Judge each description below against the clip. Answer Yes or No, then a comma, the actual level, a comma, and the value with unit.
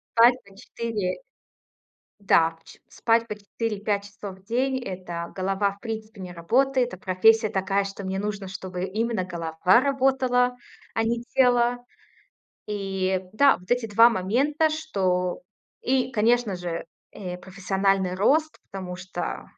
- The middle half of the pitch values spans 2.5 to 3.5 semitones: No, average, 4.2 semitones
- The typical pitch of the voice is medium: No, high, 205 Hz